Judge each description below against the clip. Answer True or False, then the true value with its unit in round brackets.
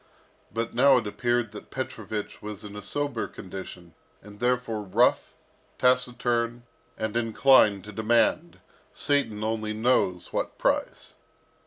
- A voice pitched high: False (115 Hz)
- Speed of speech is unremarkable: False (125 wpm)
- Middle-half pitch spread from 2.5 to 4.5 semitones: True (3.1 semitones)